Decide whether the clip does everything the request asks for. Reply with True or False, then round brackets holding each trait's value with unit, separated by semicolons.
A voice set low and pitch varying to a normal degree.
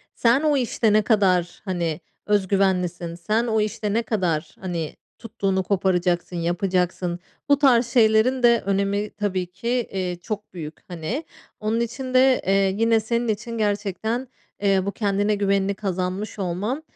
False (200 Hz; 3.7 semitones)